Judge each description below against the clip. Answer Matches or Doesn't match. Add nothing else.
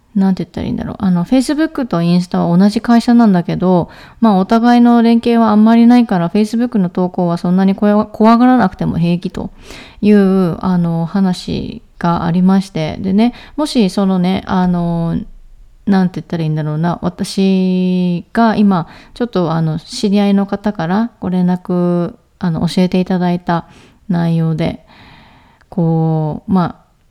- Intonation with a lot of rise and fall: Doesn't match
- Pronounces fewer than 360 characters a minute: Matches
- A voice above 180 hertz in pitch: Matches